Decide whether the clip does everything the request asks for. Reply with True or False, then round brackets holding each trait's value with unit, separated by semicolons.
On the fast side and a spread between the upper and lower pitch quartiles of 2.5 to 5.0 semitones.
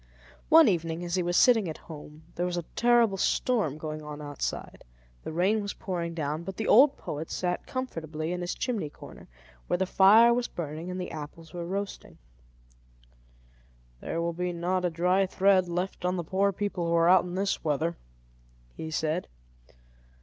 False (180 wpm; 3.2 semitones)